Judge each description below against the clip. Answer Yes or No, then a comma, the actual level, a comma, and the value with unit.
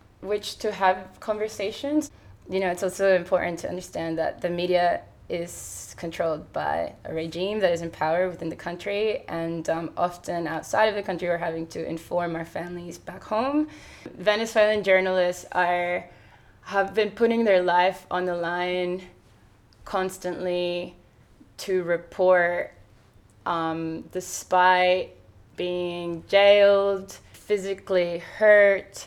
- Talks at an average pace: No, slow, 125 wpm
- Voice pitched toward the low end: No, medium, 180 Hz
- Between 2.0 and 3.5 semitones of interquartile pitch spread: Yes, narrow, 2.5 semitones